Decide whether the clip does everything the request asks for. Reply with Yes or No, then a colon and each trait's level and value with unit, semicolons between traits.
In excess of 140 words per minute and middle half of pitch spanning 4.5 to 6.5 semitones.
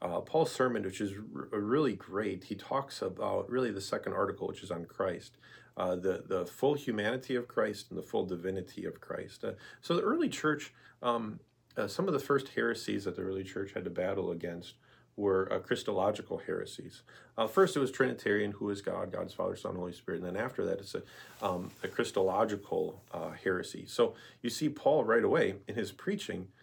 Yes: fast, 205 wpm; average, 5.3 semitones